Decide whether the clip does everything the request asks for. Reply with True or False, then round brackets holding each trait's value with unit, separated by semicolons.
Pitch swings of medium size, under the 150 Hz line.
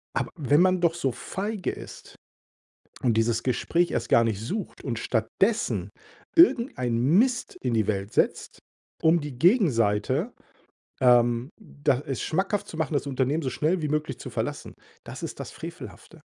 False (7.0 semitones; 140 Hz)